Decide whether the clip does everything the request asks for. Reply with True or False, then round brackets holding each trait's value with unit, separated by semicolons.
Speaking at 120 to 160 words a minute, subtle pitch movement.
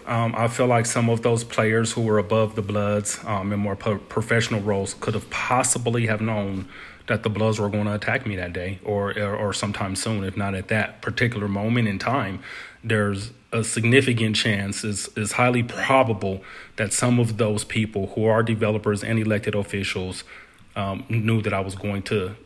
False (195 wpm; 2.1 semitones)